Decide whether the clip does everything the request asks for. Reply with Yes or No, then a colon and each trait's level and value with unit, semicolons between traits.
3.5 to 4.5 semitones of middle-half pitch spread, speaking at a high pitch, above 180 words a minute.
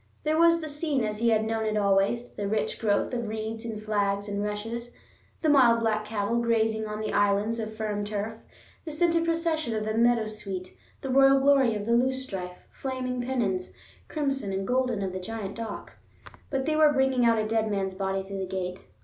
Yes: average, 4.1 semitones; high, 220 Hz; average, 200 wpm